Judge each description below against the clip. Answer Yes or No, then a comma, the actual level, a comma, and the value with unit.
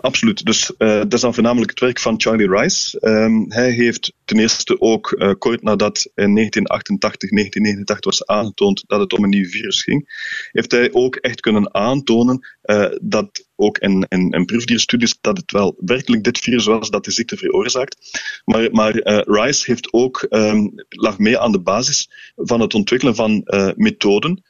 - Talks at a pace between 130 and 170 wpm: No, average, 185 wpm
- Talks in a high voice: No, low, 110 Hz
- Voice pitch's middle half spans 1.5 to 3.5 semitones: Yes, average, 3.1 semitones